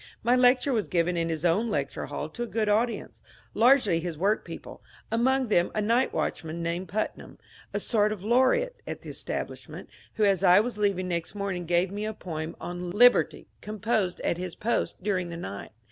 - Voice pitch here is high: Yes, high, 205 Hz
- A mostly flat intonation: No, average, 4.6 semitones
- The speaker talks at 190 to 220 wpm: Yes, average, 195 wpm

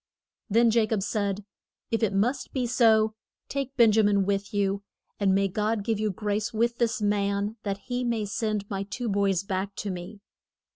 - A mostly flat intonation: Yes, narrow, 2.2 semitones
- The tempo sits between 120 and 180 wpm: No, average, 190 wpm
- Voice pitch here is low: No, high, 210 Hz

